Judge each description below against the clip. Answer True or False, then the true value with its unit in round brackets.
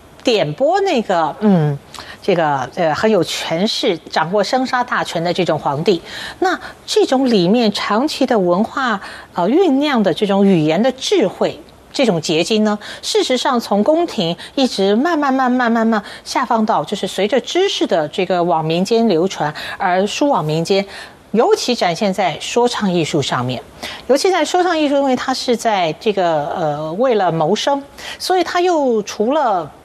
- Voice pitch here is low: False (225 Hz)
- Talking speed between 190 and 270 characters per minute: True (245 characters per minute)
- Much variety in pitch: True (7.2 semitones)